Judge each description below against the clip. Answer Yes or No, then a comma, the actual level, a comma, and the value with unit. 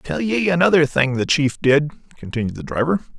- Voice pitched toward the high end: No, medium, 150 Hz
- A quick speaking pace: No, average, 190 wpm